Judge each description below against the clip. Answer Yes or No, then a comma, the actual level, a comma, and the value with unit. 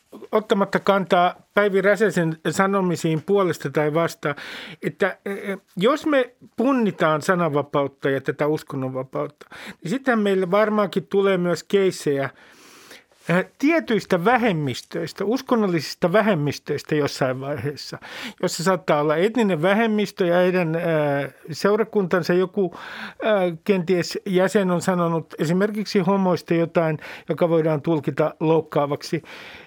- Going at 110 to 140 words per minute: No, average, 100 wpm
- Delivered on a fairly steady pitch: No, average, 4.4 semitones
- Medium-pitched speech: Yes, medium, 180 Hz